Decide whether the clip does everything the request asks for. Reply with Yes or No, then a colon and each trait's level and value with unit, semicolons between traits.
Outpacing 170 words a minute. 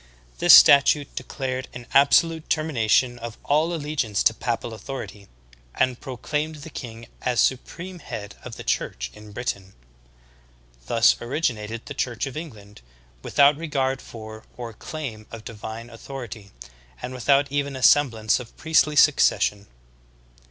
No: average, 140 wpm